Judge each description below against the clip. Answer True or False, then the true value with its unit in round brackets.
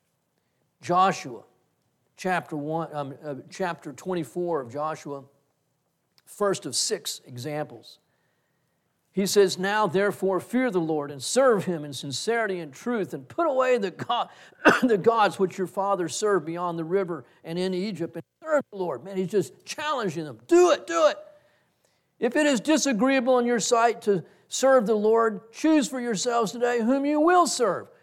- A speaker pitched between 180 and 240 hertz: True (190 Hz)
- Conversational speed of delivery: True (165 wpm)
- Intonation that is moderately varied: False (7.4 semitones)